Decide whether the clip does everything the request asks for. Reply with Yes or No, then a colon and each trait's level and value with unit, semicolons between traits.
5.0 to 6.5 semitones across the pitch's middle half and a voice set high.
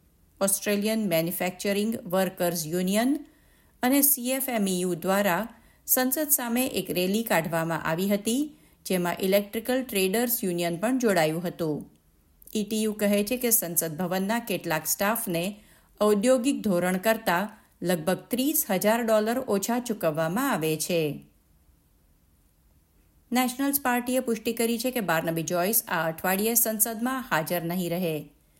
Yes: wide, 5.5 semitones; high, 200 Hz